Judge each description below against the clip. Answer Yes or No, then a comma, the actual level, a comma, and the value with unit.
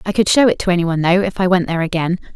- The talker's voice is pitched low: No, medium, 180 Hz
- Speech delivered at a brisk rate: Yes, fast, 330 wpm